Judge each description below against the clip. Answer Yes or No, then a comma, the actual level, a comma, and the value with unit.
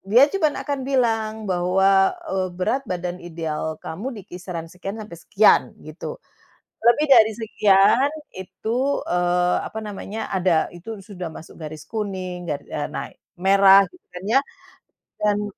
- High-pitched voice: Yes, high, 195 Hz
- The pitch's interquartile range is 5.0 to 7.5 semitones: No, average, 3.7 semitones